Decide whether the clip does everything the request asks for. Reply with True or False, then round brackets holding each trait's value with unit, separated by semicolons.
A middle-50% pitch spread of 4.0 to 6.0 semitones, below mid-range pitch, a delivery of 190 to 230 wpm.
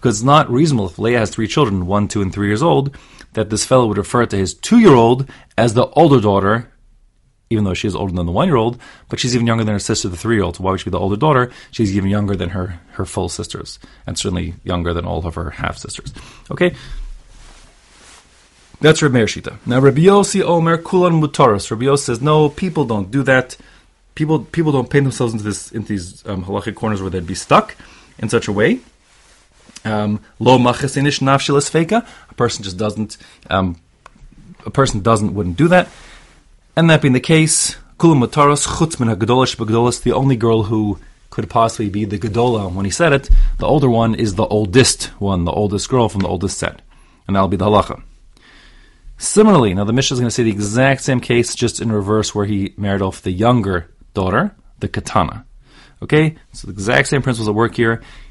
True (5.0 semitones; 115 Hz; 200 wpm)